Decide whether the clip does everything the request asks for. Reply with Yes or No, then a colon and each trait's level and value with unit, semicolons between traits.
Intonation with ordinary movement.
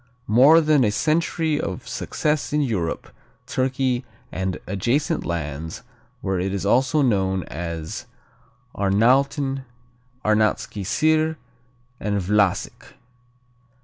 No: wide, 7.1 semitones